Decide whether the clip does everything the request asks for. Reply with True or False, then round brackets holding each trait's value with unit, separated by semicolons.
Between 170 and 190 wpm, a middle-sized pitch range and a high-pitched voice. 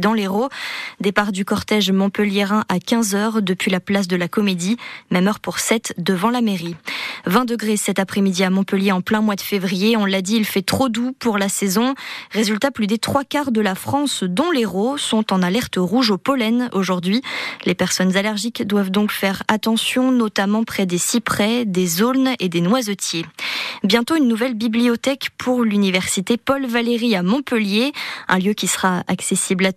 True (180 wpm; 3.5 semitones; 215 Hz)